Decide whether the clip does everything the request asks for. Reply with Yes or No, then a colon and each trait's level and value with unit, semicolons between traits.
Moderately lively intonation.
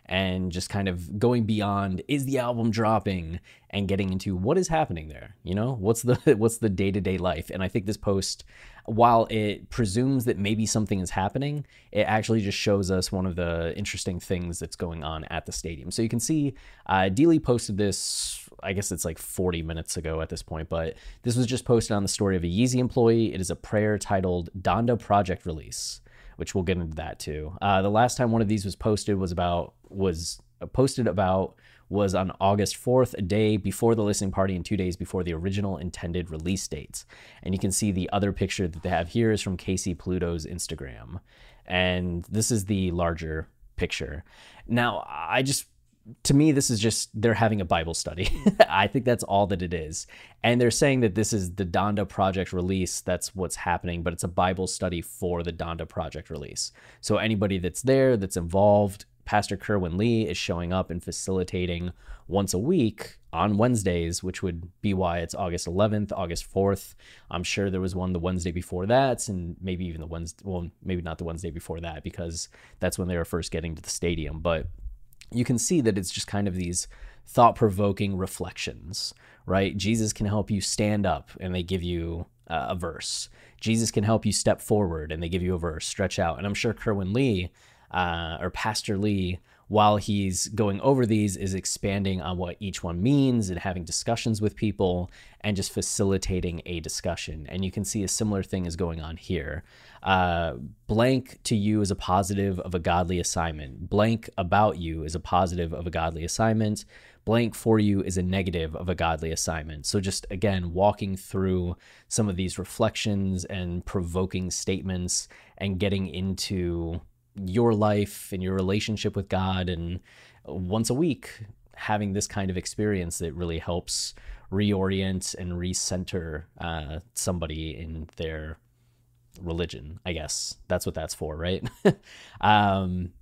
Yes: average, 3.2 semitones